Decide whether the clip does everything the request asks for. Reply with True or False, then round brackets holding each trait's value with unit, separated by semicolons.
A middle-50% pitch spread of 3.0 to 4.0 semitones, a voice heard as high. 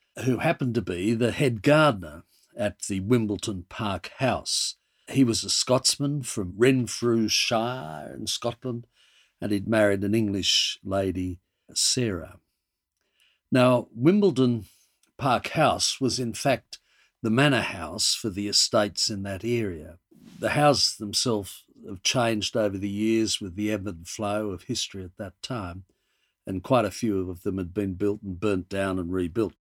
False (3.6 semitones; 105 Hz)